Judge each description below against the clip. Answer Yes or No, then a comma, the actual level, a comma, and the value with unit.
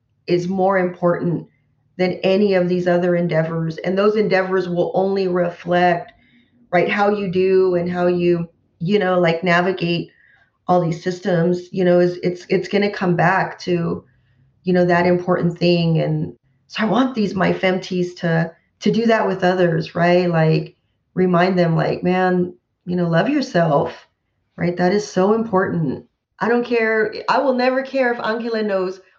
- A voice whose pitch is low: No, medium, 180 Hz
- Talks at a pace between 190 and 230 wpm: No, average, 170 wpm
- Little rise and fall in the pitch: Yes, narrow, 1.7 semitones